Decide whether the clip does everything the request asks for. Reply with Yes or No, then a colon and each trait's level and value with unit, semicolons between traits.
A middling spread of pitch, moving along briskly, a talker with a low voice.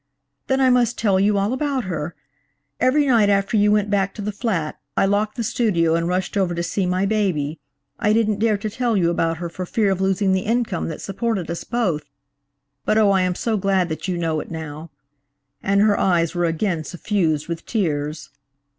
No: average, 4.0 semitones; fast, 210 wpm; high, 195 Hz